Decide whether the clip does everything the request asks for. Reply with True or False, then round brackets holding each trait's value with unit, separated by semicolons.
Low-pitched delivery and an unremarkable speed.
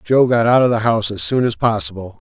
False (115 Hz; 265 wpm)